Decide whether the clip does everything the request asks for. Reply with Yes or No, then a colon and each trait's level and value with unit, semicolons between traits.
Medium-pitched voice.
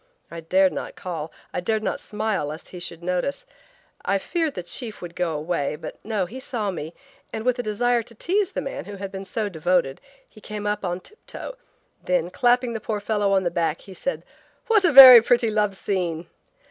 No: high, 200 Hz